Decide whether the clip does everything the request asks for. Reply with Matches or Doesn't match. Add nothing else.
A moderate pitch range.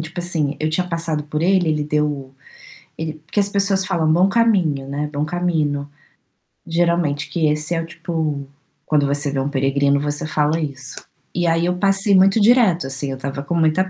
Matches